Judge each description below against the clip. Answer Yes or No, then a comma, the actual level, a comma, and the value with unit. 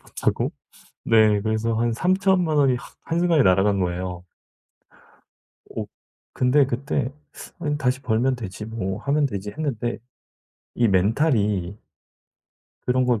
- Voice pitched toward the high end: No, low, 120 Hz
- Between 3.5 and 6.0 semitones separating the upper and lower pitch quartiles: Yes, wide, 5.4 semitones